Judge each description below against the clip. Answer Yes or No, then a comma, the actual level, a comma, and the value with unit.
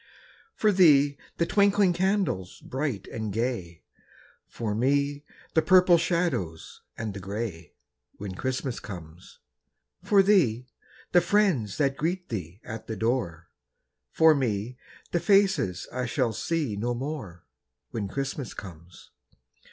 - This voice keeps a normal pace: No, slow, 125 wpm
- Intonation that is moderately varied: No, wide, 8.7 semitones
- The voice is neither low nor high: No, low, 125 Hz